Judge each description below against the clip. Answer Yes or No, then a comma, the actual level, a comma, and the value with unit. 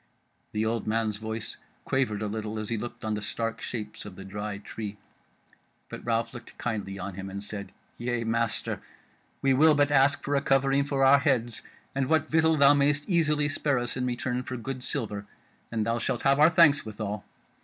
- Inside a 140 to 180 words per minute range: No, average, 200 wpm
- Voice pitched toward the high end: No, low, 120 Hz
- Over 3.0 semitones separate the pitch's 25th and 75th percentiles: Yes, average, 4.5 semitones